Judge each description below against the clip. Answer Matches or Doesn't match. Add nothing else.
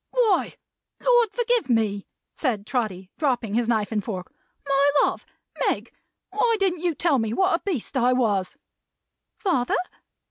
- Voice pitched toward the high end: Matches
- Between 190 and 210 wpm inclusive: Doesn't match